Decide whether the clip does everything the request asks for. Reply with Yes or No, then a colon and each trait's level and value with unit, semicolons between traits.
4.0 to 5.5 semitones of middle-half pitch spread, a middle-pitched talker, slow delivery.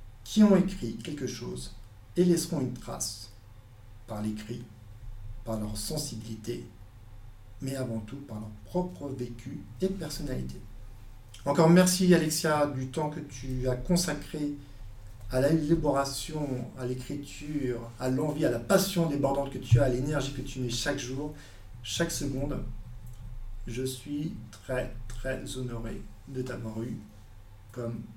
No: average, 5.1 semitones; low, 125 Hz; slow, 135 wpm